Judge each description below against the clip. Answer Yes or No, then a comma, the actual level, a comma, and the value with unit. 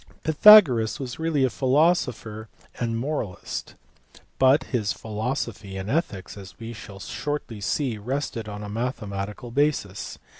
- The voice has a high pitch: No, low, 115 Hz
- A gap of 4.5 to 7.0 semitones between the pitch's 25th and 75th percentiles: Yes, average, 5.0 semitones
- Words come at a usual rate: No, slow, 125 wpm